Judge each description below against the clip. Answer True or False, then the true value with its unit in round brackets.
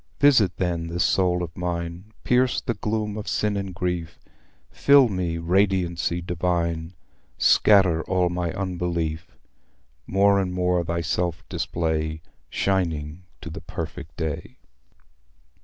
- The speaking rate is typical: False (120 wpm)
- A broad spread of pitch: False (2.4 semitones)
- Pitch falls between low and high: False (90 Hz)